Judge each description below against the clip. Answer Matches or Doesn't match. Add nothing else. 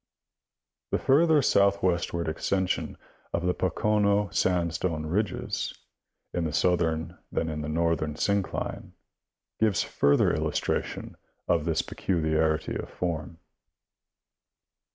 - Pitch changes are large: Doesn't match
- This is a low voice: Matches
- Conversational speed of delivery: Doesn't match